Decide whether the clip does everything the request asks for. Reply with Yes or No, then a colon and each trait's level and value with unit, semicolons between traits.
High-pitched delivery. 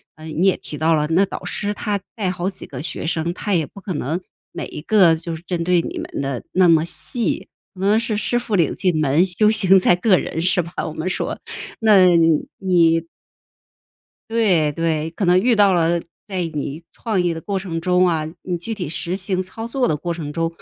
No: medium, 175 Hz